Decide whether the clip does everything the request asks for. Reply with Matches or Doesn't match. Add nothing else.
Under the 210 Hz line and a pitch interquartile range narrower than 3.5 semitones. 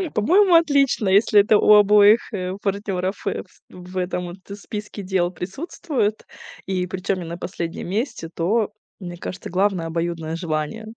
Matches